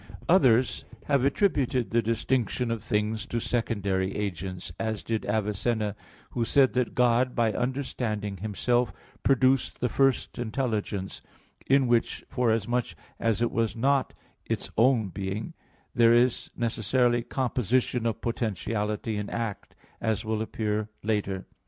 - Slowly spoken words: Yes, slow, 130 wpm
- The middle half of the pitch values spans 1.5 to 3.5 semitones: Yes, average, 2.8 semitones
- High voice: No, low, 115 Hz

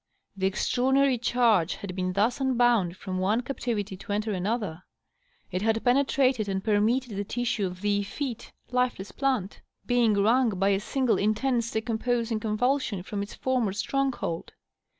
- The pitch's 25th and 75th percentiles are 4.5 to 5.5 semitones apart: No, average, 3.8 semitones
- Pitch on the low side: No, high, 220 Hz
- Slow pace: No, average, 150 wpm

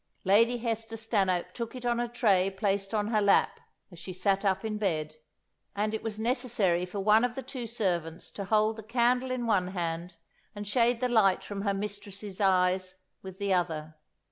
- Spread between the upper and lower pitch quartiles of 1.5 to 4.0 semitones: Yes, average, 3.5 semitones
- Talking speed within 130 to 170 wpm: No, average, 195 wpm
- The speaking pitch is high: Yes, high, 205 Hz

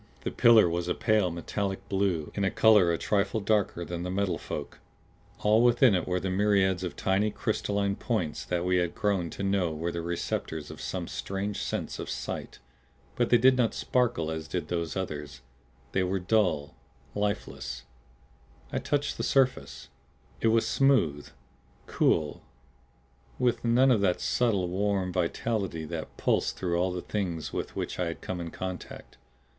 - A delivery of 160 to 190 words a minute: Yes, average, 165 wpm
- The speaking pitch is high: No, very low, 95 Hz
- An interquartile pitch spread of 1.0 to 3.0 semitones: No, average, 3.6 semitones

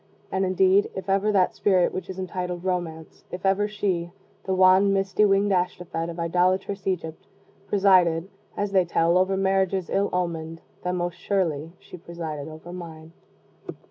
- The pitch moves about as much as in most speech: No, narrow, 2.2 semitones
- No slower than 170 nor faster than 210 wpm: No, average, 155 wpm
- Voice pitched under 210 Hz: Yes, medium, 185 Hz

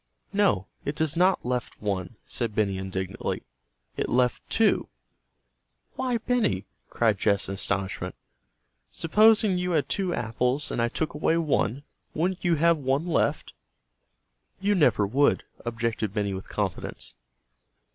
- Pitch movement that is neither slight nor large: No, wide, 8.9 semitones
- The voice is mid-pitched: No, low, 130 Hz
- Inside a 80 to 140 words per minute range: Yes, slow, 135 wpm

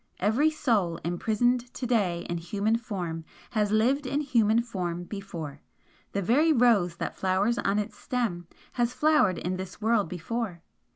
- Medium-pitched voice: No, high, 210 Hz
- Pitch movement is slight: No, average, 5.2 semitones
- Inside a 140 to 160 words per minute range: Yes, average, 155 wpm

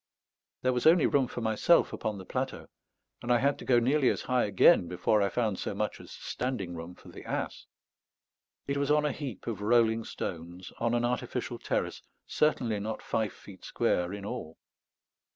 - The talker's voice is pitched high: No, low, 115 Hz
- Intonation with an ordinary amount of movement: Yes, average, 4.3 semitones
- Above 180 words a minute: Yes, average, 190 wpm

